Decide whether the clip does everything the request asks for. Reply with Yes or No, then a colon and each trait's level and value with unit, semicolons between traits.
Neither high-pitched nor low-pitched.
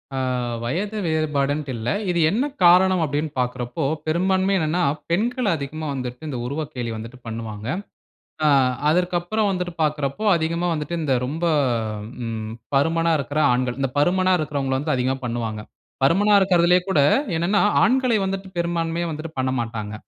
Yes: medium, 155 Hz